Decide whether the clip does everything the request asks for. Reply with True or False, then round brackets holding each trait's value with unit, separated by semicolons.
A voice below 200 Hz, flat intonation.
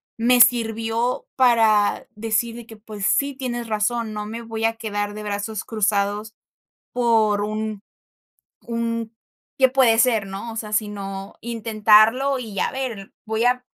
False (225 Hz; 2.0 semitones)